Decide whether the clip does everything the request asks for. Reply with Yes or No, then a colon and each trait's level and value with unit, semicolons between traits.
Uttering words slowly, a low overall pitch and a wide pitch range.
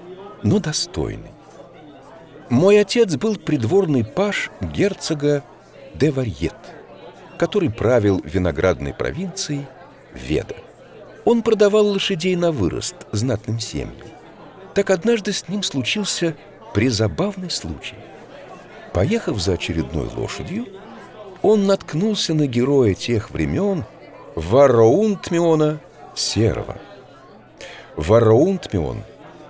No: slow, 85 wpm; medium, 160 Hz; wide, 7.4 semitones